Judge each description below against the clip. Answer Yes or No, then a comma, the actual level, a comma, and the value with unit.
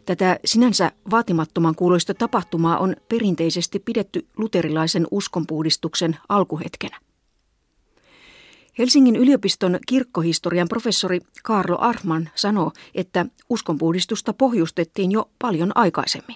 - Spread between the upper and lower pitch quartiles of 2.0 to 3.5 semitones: No, average, 5.1 semitones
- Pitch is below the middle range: No, medium, 185 Hz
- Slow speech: Yes, slow, 90 wpm